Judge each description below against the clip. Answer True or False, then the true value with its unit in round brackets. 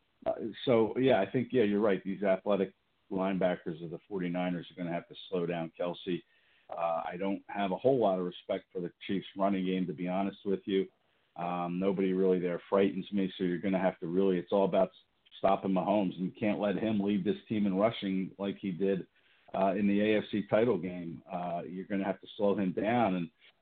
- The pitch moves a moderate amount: False (1.8 semitones)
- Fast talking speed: True (225 wpm)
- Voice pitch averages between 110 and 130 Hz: False (95 Hz)